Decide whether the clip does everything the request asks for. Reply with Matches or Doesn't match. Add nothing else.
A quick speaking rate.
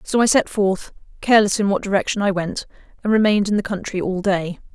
Matches